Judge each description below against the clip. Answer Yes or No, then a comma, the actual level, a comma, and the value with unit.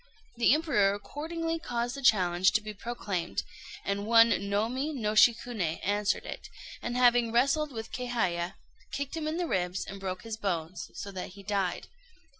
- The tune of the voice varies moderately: Yes, average, 4.2 semitones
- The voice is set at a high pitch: Yes, high, 220 Hz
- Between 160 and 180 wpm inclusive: Yes, average, 165 wpm